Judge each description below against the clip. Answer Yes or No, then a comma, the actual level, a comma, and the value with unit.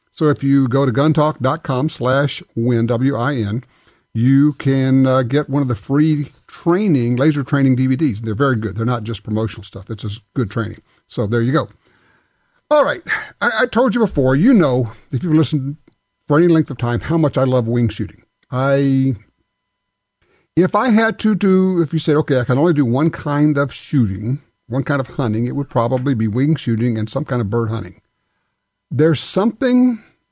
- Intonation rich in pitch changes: No, average, 4.4 semitones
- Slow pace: No, average, 190 wpm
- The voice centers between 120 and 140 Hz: Yes, low, 135 Hz